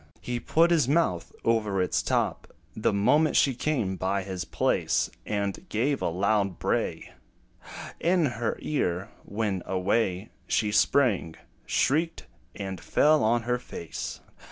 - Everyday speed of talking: No, slow, 130 wpm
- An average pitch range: No, wide, 6.1 semitones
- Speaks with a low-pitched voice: Yes, low, 110 Hz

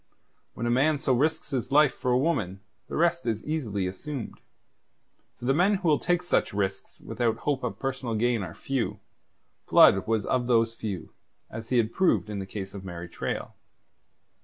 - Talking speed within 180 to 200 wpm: Yes, average, 185 wpm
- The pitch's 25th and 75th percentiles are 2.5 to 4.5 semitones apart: No, wide, 5.6 semitones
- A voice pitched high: No, low, 120 Hz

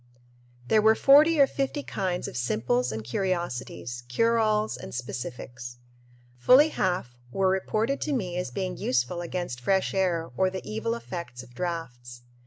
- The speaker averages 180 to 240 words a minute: No, average, 155 wpm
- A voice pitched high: No, medium, 180 Hz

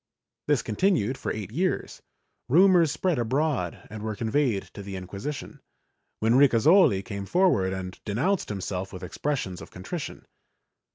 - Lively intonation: Yes, wide, 7.4 semitones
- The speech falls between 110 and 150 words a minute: Yes, average, 140 wpm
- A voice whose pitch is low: Yes, low, 115 Hz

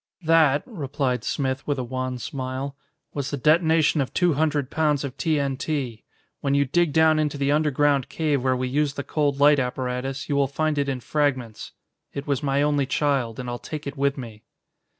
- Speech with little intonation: Yes, narrow, 2.3 semitones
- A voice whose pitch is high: No, medium, 140 Hz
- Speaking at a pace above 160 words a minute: Yes, average, 190 wpm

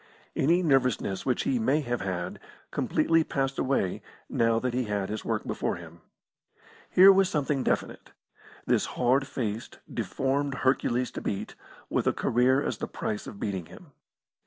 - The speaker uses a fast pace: No, average, 160 wpm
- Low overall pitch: Yes, low, 130 Hz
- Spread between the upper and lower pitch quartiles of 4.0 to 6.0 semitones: Yes, average, 5.1 semitones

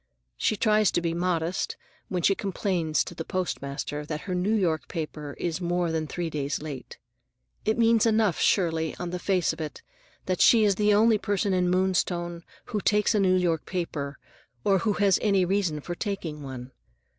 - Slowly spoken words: No, average, 185 wpm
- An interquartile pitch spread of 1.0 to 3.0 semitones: No, average, 3.8 semitones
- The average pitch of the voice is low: No, medium, 180 Hz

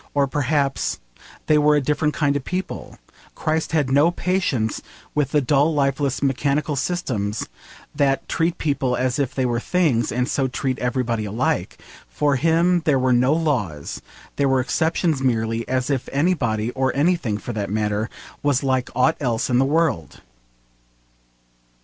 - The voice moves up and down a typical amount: Yes, average, 3.4 semitones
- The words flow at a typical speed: Yes, average, 155 wpm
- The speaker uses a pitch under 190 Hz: Yes, low, 135 Hz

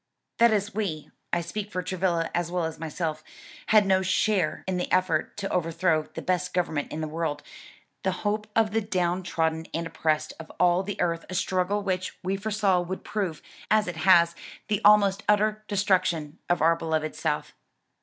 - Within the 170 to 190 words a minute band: Yes, average, 185 wpm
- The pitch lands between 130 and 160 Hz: No, medium, 180 Hz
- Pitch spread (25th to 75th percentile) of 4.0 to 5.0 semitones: No, average, 3.4 semitones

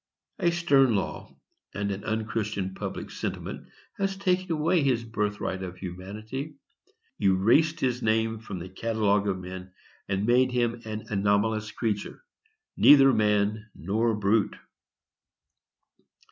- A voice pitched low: Yes, low, 110 Hz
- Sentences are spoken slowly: Yes, slow, 120 wpm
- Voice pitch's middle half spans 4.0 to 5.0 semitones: Yes, average, 4.3 semitones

